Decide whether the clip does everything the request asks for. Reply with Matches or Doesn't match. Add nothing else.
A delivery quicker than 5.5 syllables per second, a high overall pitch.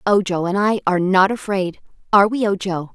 Matches